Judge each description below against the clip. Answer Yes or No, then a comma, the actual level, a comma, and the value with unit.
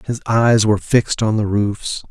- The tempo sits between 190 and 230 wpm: Yes, average, 200 wpm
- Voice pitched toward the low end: Yes, low, 110 Hz